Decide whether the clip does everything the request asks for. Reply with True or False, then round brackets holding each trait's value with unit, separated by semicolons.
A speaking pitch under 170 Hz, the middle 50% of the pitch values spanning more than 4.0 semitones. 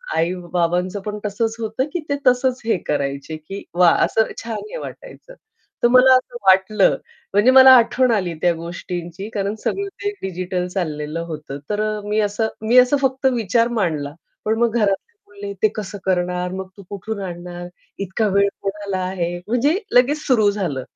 False (200 Hz; 4.5 semitones)